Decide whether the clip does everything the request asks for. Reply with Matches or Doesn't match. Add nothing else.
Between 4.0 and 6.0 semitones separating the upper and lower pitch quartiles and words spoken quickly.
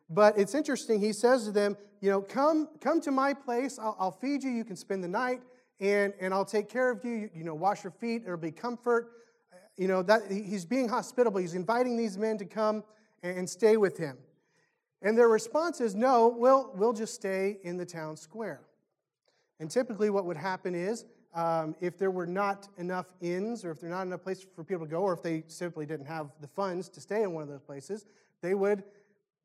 Matches